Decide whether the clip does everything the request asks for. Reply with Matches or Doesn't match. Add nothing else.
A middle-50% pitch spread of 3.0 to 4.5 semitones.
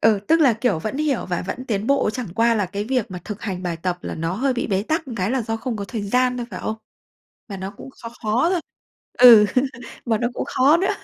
Matches